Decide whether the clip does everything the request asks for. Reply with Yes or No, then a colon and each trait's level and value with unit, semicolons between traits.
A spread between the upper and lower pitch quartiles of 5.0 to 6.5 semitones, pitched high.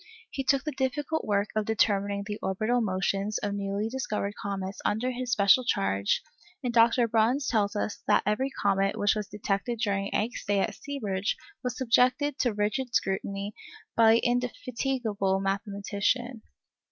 No: average, 3.7 semitones; high, 215 Hz